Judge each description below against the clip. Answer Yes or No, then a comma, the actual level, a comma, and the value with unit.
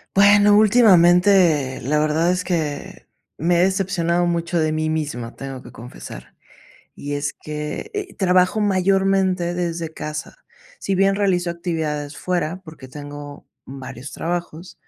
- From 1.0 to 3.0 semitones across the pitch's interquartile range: No, average, 3.9 semitones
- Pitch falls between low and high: Yes, medium, 170 Hz